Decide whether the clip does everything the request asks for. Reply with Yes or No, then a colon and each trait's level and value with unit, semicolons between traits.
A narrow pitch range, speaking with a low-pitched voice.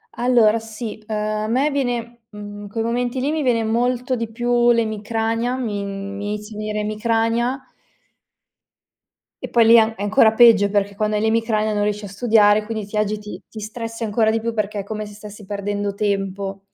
No: narrow, 1.9 semitones; high, 220 Hz